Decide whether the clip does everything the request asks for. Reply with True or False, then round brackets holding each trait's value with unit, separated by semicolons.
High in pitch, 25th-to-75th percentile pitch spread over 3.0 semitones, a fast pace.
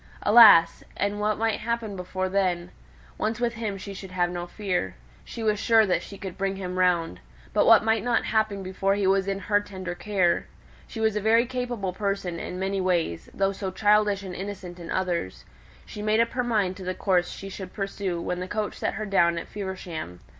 False (195 Hz; 2.7 semitones; 210 wpm)